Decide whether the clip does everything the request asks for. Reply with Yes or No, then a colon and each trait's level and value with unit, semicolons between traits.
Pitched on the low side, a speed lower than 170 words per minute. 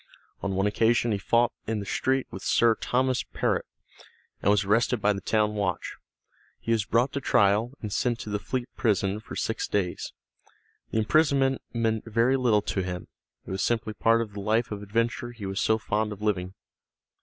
No: low, 110 Hz; average, 190 wpm